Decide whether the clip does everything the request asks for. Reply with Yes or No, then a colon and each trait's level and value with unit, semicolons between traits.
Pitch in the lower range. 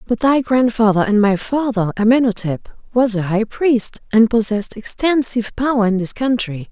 No: high, 225 Hz